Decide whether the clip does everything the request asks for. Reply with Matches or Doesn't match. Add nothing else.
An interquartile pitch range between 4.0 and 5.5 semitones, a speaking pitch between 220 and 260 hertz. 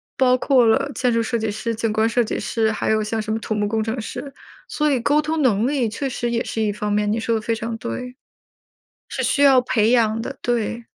Doesn't match